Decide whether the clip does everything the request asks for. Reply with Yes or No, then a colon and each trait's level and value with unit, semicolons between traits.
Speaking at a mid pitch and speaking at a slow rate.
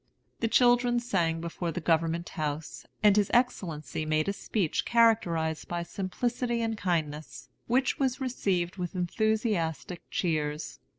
Yes: medium, 180 Hz; slow, 130 wpm